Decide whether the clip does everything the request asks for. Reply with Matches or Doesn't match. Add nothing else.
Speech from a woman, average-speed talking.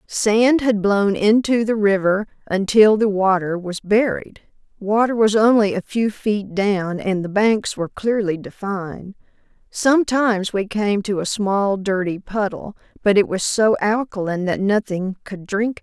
Matches